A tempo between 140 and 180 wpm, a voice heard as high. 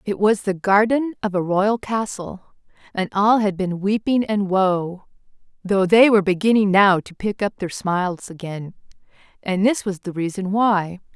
Yes: average, 170 wpm; high, 200 Hz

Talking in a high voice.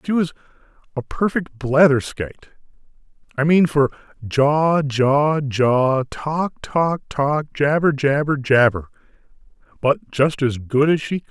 No: medium, 145 Hz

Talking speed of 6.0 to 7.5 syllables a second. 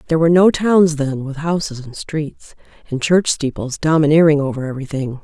No: 5.5 syllables/s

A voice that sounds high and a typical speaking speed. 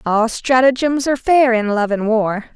Yes: high, 240 Hz; average, 190 wpm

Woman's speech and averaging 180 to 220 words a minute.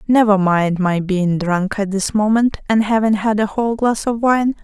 Yes: female; fast, 205 wpm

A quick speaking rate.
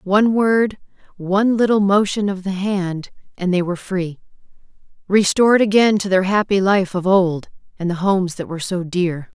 No: average, 170 wpm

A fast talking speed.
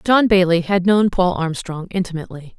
No: average, 165 wpm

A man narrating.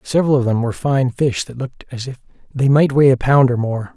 Yes: male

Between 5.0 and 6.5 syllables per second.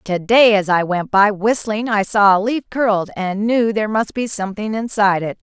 Yes: 5.2 syllables/s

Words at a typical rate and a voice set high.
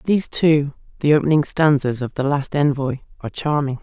No: average, 175 wpm; medium, 145 Hz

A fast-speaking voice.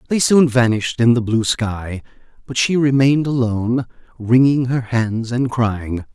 No: average, 155 wpm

